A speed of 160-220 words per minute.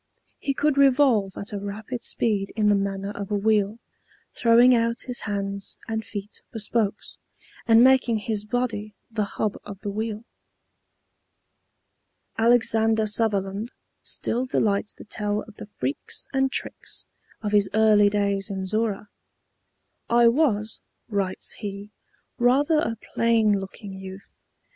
No: slow, 135 wpm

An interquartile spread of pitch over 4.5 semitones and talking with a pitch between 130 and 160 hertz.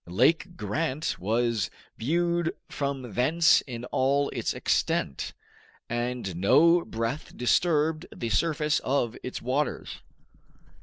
Yes: average, 5.1 semitones; low, 135 Hz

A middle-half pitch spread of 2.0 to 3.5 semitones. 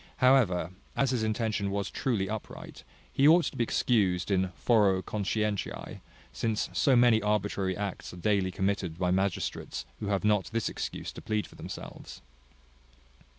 Yes: average, 2.8 semitones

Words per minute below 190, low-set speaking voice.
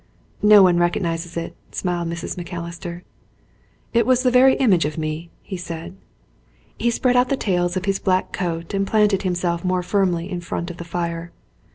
No: average, 180 wpm; medium, 180 Hz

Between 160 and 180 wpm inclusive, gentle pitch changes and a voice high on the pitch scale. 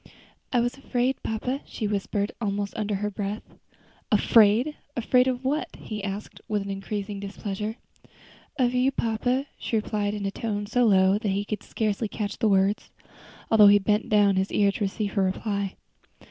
Yes: average, 170 wpm; narrow, 2.2 semitones; high, 210 Hz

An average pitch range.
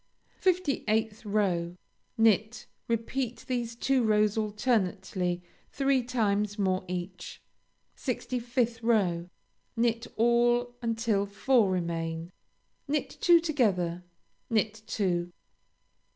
Yes: average, 4.3 semitones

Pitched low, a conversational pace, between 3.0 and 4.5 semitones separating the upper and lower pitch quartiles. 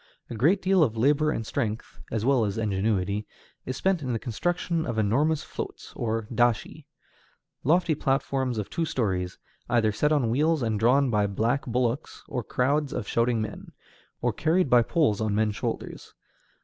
No: low, 120 Hz; average, 170 wpm; average, 5.2 semitones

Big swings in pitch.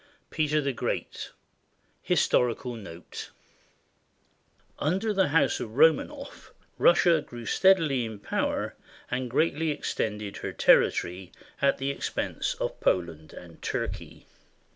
Yes: wide, 6.9 semitones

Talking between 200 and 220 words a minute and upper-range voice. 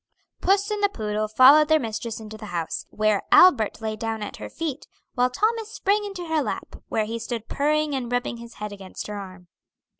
Yes: fast, 205 wpm; high, 235 Hz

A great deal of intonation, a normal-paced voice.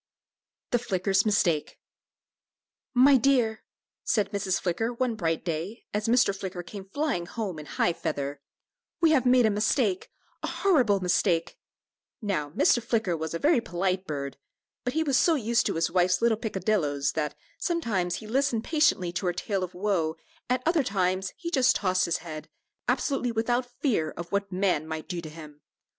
Yes: wide, 5.8 semitones; average, 175 wpm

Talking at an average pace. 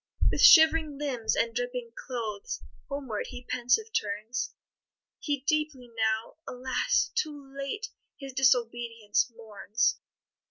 No: slow, 110 wpm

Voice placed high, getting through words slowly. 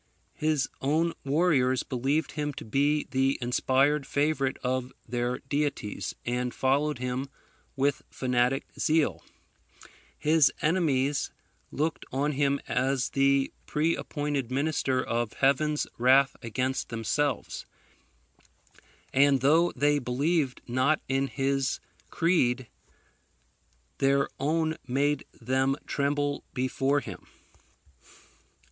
No: low, 135 Hz; slow, 100 wpm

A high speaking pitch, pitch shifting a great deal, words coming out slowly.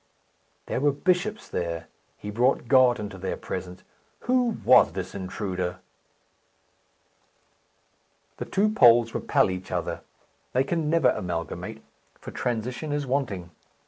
No: low, 120 Hz; wide, 7.5 semitones; slow, 120 wpm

